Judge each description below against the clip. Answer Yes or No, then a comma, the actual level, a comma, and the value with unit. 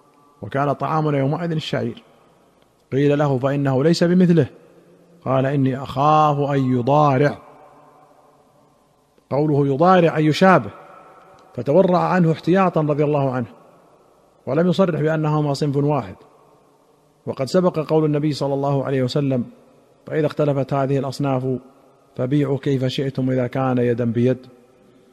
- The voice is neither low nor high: Yes, medium, 145 Hz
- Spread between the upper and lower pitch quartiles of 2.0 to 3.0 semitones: Yes, narrow, 2.5 semitones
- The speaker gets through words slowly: No, average, 115 wpm